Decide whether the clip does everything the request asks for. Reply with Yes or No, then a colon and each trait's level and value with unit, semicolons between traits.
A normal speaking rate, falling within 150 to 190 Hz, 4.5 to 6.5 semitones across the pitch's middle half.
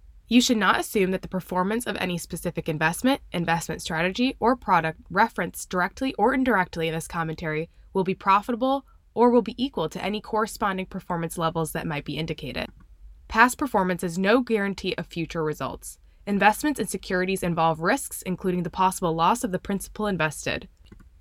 Yes: average, 165 wpm; medium, 185 Hz; average, 4.9 semitones